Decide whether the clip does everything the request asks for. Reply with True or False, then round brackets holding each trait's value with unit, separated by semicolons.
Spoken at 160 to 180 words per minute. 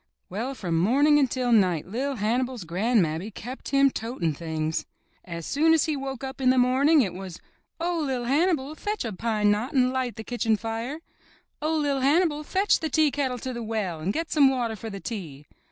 False (200 wpm)